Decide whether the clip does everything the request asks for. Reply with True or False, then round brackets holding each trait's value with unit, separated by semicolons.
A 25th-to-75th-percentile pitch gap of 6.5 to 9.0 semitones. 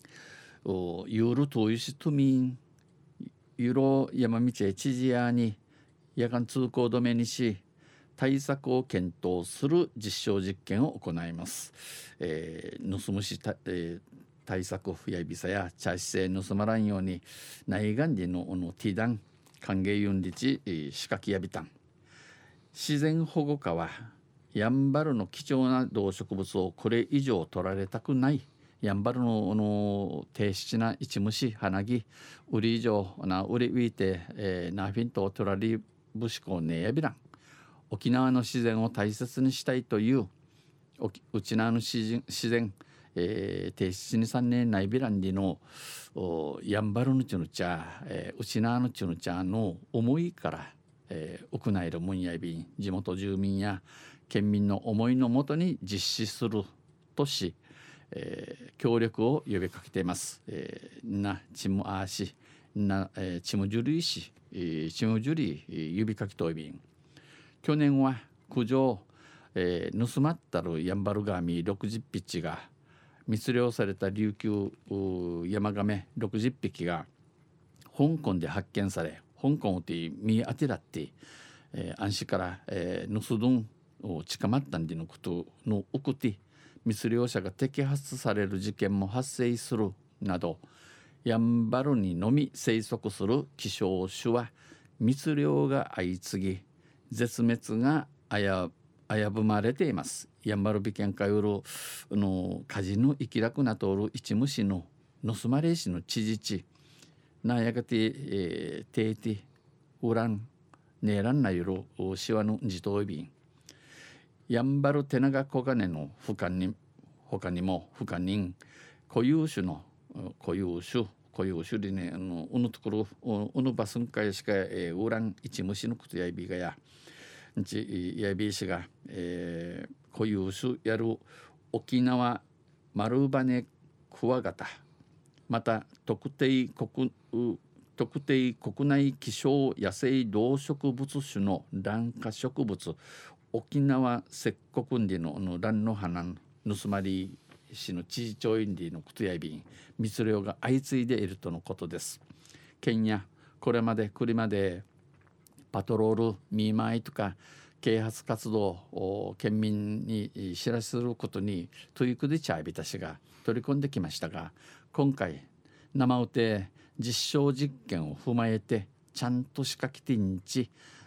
False (5.1 semitones)